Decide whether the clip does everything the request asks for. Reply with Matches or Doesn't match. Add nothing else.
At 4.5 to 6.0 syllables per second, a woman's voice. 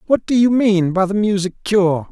Doesn't match